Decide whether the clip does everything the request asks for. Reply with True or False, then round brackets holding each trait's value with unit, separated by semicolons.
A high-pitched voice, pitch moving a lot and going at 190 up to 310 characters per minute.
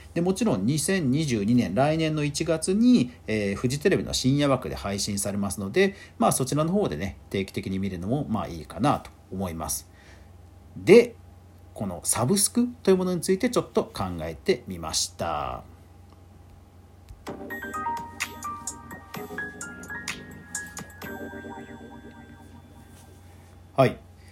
False (95 Hz; 8.6 semitones; 210 characters per minute)